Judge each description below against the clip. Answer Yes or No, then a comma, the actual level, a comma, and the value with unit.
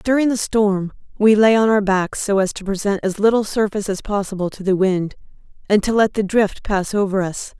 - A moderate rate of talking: No, fast, 220 wpm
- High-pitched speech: Yes, high, 205 Hz